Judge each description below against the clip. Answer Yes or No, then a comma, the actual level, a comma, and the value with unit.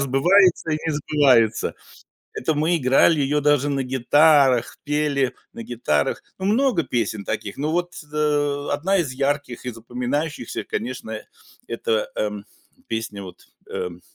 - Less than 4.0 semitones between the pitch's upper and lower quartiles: No, average, 4.4 semitones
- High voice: No, medium, 140 Hz